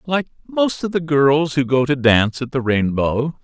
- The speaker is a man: Yes, male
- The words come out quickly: Yes, fast, 210 wpm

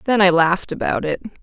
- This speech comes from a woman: Yes, female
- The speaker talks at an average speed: No, fast, 210 wpm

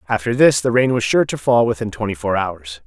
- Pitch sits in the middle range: No, low, 110 Hz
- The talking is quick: Yes, fast, 250 wpm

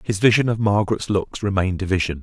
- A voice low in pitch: Yes, low, 100 Hz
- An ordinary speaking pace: No, fast, 215 wpm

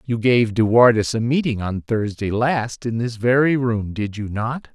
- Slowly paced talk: No, average, 200 wpm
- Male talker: Yes, male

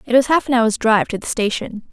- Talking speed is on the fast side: Yes, fast, 280 wpm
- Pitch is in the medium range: No, high, 235 Hz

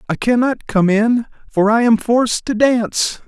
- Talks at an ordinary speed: Yes, average, 185 wpm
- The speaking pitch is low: No, high, 230 Hz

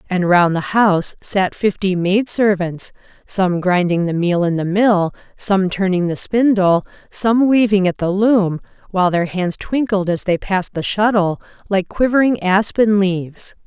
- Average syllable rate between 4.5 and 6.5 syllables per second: No, 4.3 syllables/s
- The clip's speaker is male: No, female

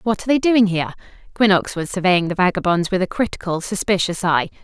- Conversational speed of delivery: Yes, average, 195 wpm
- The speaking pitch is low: No, high, 190 Hz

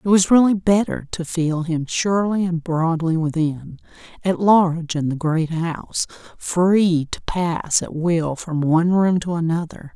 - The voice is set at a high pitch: No, medium, 170 Hz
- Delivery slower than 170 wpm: Yes, average, 155 wpm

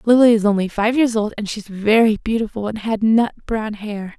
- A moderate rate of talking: No, fast, 230 wpm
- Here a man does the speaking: No, female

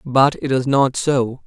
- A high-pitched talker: No, low, 135 Hz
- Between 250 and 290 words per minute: No, fast, 205 wpm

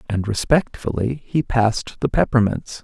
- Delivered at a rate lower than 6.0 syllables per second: Yes, 4.7 syllables/s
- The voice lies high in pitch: No, low, 115 Hz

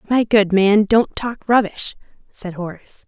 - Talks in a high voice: Yes, high, 205 Hz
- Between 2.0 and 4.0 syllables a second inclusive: No, 4.5 syllables/s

